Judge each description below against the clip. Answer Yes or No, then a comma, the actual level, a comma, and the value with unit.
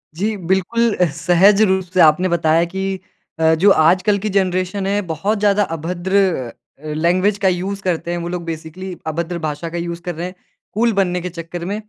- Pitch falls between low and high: Yes, medium, 180 Hz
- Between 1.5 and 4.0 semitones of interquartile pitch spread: Yes, narrow, 2.6 semitones